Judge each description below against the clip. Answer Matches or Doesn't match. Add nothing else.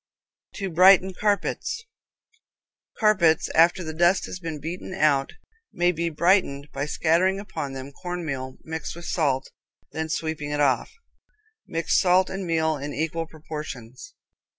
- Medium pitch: Matches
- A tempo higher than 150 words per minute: Doesn't match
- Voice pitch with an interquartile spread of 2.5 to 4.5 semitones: Matches